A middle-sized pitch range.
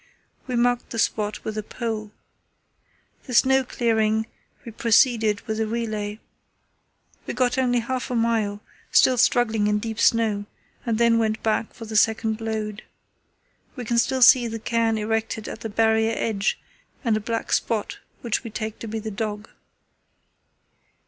No: narrow, 1.5 semitones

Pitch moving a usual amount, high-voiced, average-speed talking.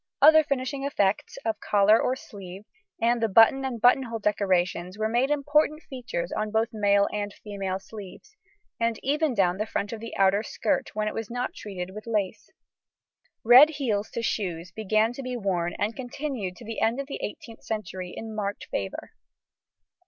Yes: average, 3.6 semitones; high, 220 Hz; average, 175 wpm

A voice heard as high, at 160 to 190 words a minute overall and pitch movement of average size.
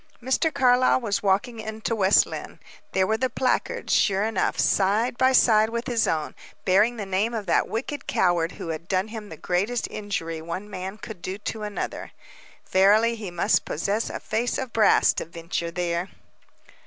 Yes: high, 210 Hz; average, 180 wpm; average, 3.8 semitones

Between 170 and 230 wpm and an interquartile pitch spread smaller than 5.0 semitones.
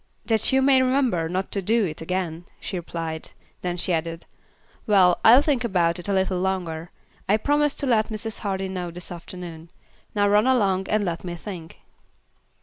Yes: average, 180 wpm; average, 4.1 semitones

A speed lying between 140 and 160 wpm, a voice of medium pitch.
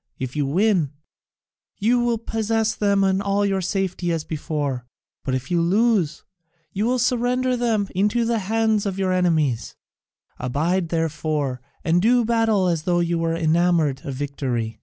Yes: average, 155 wpm; medium, 180 Hz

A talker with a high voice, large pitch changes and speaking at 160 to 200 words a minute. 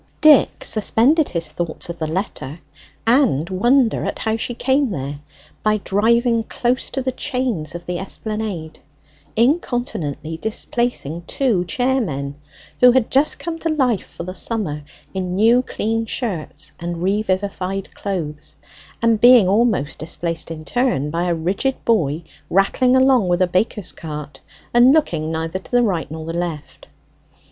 No: high, 200 Hz; wide, 6.6 semitones; average, 150 wpm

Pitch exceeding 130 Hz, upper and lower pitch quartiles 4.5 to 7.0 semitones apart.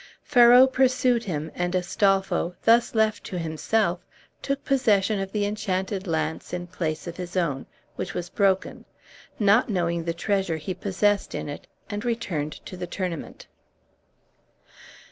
No: high, 190 Hz; average, 3.8 semitones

